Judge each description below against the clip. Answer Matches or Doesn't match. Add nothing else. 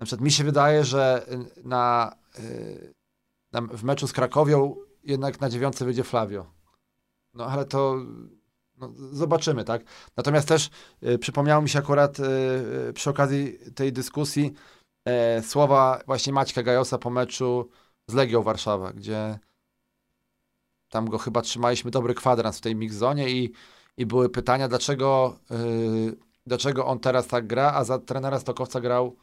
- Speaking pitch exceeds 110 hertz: Matches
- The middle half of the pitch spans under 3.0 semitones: Matches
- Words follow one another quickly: Doesn't match